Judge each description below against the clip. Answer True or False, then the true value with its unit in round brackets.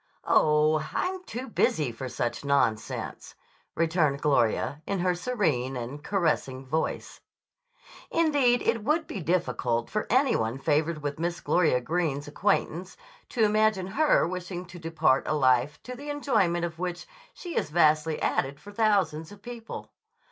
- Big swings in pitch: True (6.1 semitones)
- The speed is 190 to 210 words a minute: False (150 wpm)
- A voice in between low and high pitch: True (170 Hz)